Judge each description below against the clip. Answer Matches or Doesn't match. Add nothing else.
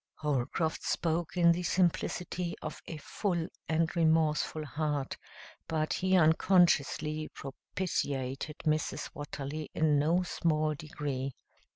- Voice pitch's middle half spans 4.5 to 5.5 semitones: Doesn't match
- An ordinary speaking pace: Doesn't match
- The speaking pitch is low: Doesn't match